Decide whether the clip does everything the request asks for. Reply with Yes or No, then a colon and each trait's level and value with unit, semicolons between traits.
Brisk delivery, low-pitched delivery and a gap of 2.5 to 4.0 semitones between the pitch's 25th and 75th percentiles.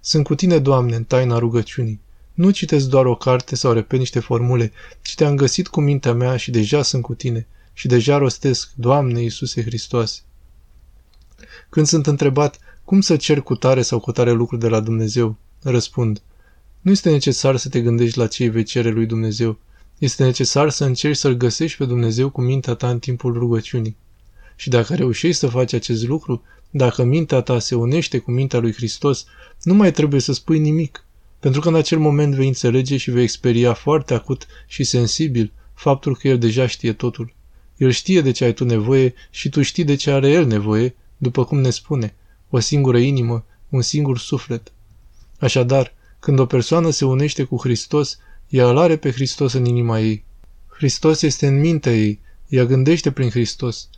Yes: fast, 185 wpm; low, 125 Hz; average, 3.4 semitones